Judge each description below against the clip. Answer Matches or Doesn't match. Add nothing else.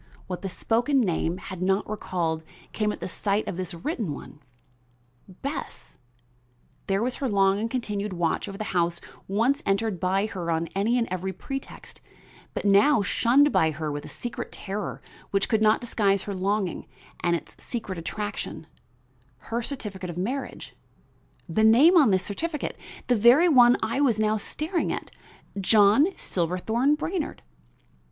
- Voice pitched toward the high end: Matches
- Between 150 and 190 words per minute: Matches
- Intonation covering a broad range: Doesn't match